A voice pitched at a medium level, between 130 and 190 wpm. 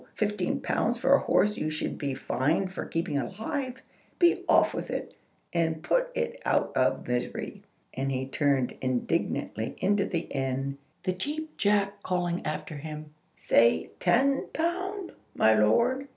Yes: medium, 175 Hz; average, 150 wpm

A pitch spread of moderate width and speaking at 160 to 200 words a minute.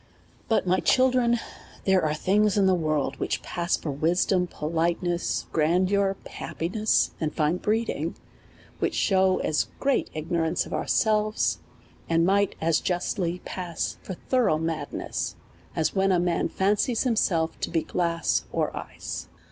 No: average, 3.5 semitones; average, 140 wpm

